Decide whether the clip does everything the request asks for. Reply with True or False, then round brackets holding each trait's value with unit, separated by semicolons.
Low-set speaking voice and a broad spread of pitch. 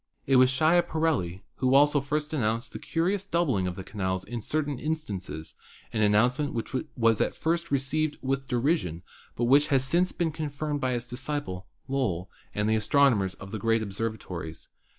True (130 Hz; 5.9 semitones)